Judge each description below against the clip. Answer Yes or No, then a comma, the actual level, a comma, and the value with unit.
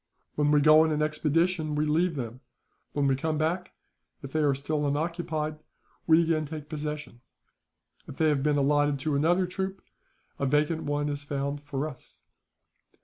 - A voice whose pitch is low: No, medium, 150 Hz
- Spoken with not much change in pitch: Yes, narrow, 1.6 semitones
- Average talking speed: Yes, average, 170 wpm